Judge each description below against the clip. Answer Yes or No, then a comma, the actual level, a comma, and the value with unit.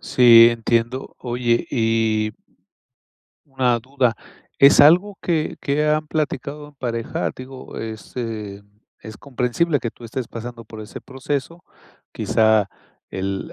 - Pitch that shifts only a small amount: No, average, 3.8 semitones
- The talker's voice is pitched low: Yes, low, 120 Hz